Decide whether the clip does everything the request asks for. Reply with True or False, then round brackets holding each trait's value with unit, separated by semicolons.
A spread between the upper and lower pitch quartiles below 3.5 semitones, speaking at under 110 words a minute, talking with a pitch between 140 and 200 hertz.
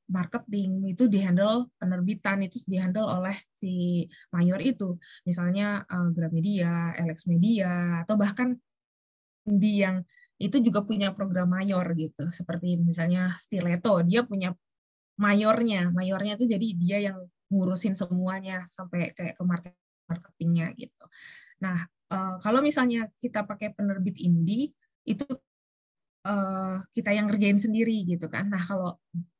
False (2.8 semitones; 125 wpm; 190 Hz)